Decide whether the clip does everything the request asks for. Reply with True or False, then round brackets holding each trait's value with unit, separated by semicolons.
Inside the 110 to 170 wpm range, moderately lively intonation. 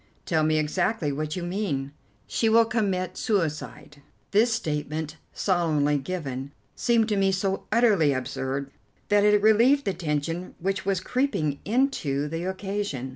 False (140 wpm; 5.7 semitones)